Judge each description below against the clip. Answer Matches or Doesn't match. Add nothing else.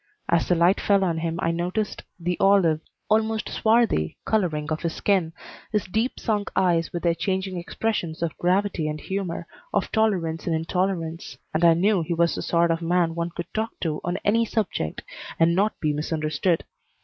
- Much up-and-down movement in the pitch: Doesn't match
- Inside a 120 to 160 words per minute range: Doesn't match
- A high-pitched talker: Doesn't match